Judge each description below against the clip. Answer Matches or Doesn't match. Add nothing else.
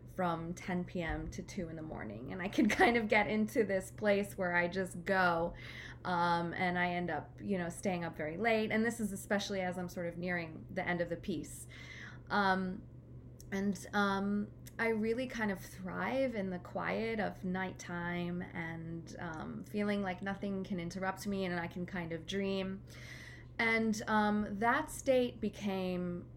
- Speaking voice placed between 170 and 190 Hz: Matches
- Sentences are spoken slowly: Doesn't match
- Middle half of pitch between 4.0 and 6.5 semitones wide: Doesn't match